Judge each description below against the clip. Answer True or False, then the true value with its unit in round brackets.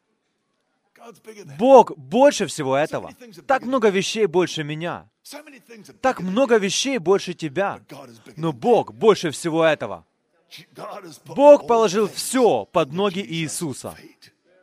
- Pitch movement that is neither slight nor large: False (6.2 semitones)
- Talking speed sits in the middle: False (105 wpm)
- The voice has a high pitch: True (195 Hz)